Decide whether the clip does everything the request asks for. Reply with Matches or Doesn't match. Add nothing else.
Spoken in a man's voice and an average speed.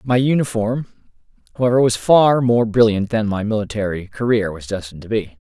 Matches